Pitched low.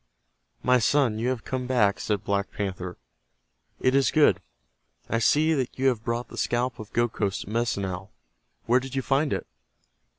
Yes: low, 120 Hz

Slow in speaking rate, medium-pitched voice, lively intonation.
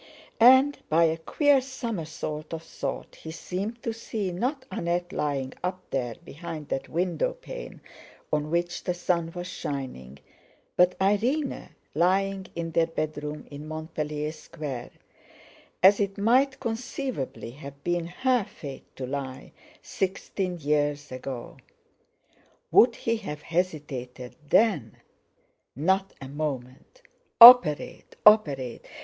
Yes: slow, 120 wpm; medium, 170 Hz; wide, 5.8 semitones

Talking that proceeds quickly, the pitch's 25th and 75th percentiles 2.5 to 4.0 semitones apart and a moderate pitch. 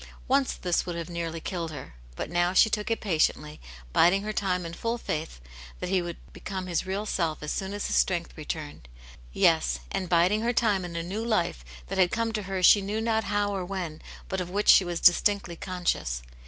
Yes: fast, 215 wpm; average, 3.5 semitones; medium, 180 Hz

